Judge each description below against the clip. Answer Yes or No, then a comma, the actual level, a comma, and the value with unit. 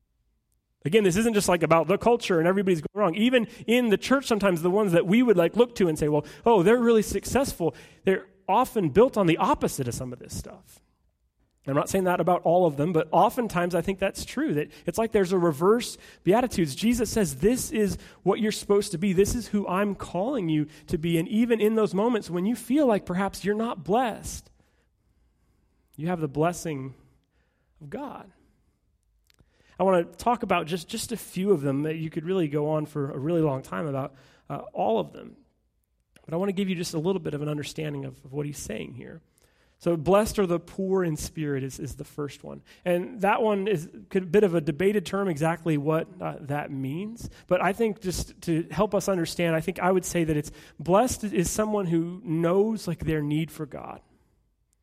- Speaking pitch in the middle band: Yes, medium, 180 Hz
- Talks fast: Yes, fast, 215 wpm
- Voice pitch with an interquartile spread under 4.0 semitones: No, average, 4.5 semitones